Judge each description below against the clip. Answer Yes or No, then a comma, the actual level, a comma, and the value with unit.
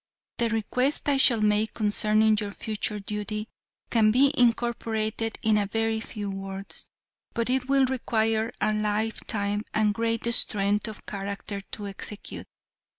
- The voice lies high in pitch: Yes, high, 215 Hz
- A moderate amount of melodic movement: No, narrow, 1.6 semitones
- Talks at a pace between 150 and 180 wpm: No, average, 140 wpm